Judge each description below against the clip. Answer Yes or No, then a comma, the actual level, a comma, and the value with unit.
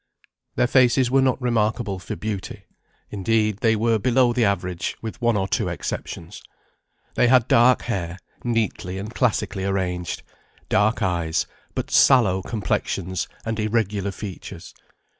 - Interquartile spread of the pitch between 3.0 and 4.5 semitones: Yes, average, 3.8 semitones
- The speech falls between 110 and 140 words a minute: Yes, slow, 135 wpm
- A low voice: Yes, low, 110 Hz